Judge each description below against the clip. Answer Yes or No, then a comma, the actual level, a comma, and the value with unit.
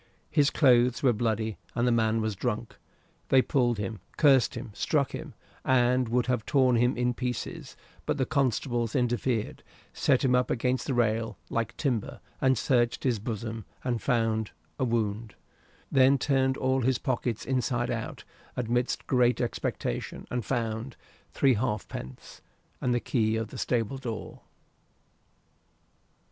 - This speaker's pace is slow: No, average, 145 wpm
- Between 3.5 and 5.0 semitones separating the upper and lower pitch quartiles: No, narrow, 2.4 semitones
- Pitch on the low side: Yes, low, 120 Hz